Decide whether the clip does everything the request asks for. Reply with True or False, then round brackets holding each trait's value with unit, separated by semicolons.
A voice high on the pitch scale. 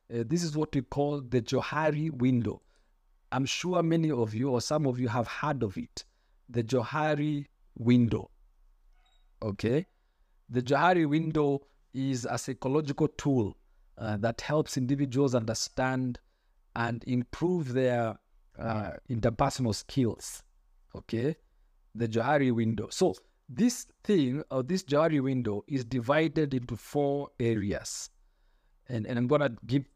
False (130 Hz)